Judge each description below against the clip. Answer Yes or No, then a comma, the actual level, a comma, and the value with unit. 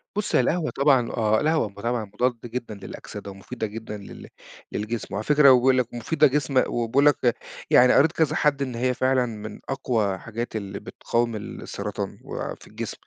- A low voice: Yes, low, 120 Hz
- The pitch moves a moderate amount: Yes, average, 3.7 semitones